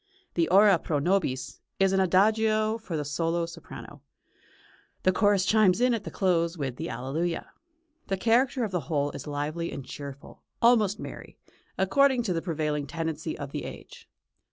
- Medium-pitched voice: Yes, medium, 175 Hz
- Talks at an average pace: Yes, average, 165 wpm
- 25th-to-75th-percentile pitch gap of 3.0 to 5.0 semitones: No, wide, 5.6 semitones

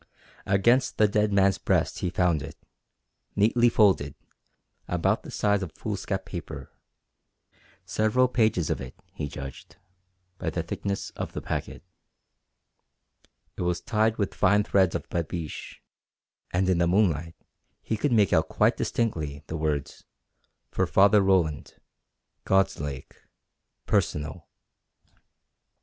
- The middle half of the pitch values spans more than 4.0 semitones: Yes, average, 4.7 semitones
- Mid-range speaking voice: No, very low, 95 Hz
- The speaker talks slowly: Yes, slow, 125 wpm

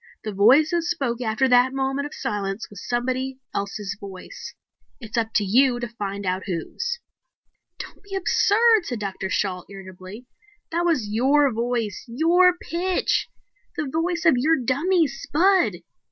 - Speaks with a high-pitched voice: Yes, very high, 250 Hz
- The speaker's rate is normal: Yes, average, 150 wpm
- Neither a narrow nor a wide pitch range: No, wide, 7.9 semitones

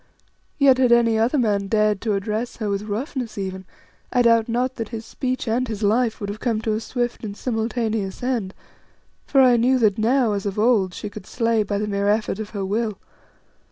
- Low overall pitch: No, high, 220 Hz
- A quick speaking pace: Yes, fast, 210 wpm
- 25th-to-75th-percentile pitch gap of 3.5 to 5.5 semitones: No, average, 2.8 semitones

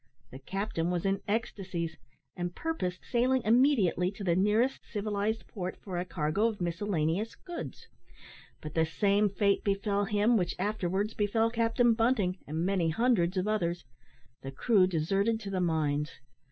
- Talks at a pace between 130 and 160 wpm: Yes, average, 155 wpm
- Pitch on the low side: No, high, 195 Hz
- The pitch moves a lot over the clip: No, average, 3.9 semitones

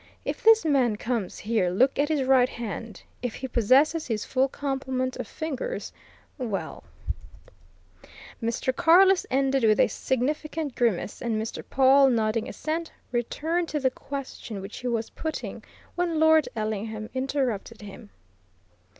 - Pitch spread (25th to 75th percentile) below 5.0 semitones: Yes, average, 4.5 semitones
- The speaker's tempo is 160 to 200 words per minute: No, average, 140 wpm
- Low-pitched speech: No, very high, 255 Hz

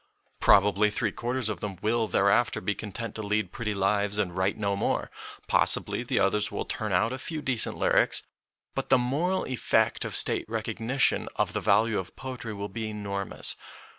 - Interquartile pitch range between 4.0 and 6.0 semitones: No, average, 2.7 semitones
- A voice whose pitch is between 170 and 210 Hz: No, low, 105 Hz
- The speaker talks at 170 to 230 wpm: Yes, average, 180 wpm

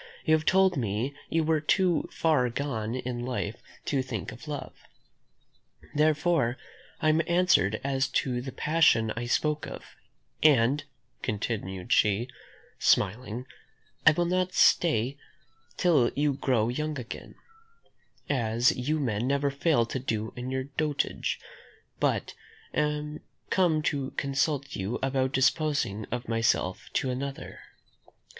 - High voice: No, low, 135 Hz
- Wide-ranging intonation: No, average, 4.2 semitones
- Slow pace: Yes, slow, 130 wpm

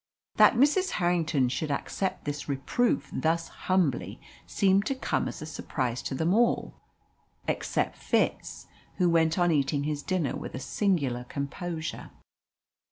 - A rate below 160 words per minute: Yes, average, 140 wpm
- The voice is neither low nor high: Yes, medium, 160 Hz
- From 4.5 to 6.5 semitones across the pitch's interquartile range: Yes, average, 4.8 semitones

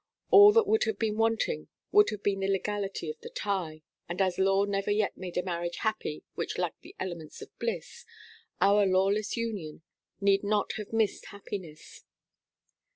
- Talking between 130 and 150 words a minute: No, average, 170 wpm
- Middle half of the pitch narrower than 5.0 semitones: Yes, average, 3.0 semitones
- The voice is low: No, high, 200 Hz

